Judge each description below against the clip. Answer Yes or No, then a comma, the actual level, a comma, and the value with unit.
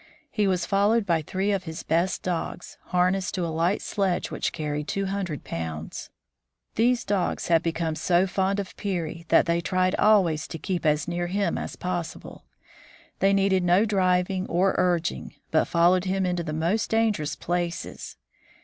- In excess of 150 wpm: Yes, average, 165 wpm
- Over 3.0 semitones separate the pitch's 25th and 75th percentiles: No, narrow, 2.6 semitones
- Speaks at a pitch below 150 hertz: No, medium, 180 Hz